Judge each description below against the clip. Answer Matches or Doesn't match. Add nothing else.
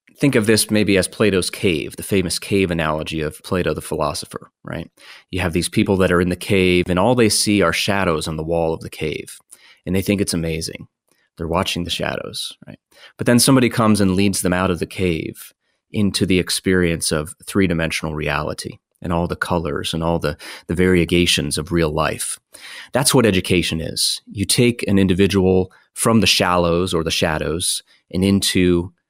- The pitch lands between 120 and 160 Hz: Doesn't match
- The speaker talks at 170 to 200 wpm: Matches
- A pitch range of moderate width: Matches